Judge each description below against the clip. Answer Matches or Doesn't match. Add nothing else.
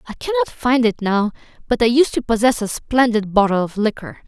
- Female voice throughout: Matches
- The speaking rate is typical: Doesn't match